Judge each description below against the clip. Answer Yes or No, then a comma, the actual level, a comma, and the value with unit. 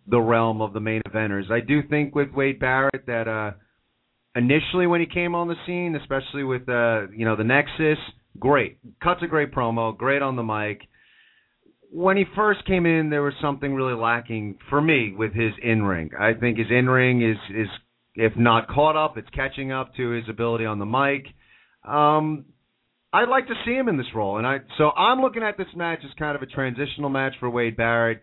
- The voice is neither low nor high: No, low, 130 Hz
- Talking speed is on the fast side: Yes, fast, 210 wpm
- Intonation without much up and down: No, average, 4.8 semitones